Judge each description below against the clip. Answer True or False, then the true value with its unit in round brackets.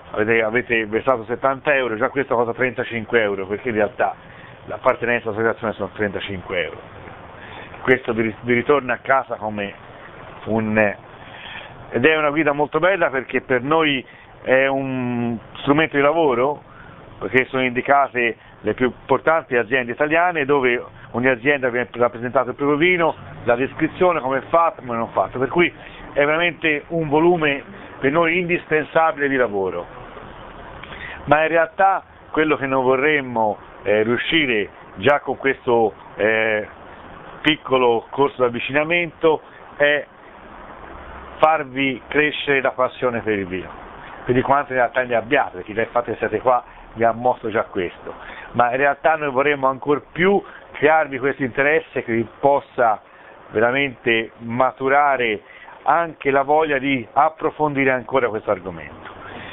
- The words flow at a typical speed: True (140 wpm)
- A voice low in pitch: True (130 Hz)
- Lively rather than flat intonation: False (4.0 semitones)